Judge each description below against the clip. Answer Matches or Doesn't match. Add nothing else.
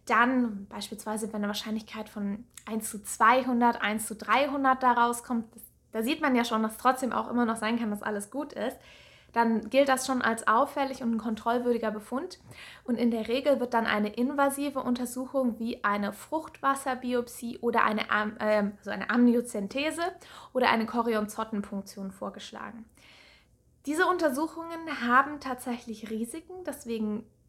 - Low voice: Doesn't match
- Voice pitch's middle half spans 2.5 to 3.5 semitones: Matches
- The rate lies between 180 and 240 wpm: Doesn't match